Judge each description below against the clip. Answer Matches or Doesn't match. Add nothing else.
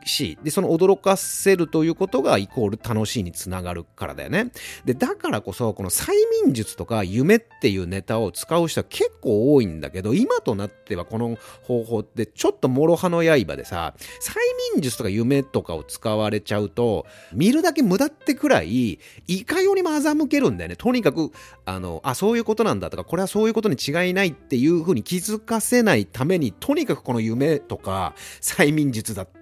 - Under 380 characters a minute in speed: Doesn't match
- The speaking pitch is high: Doesn't match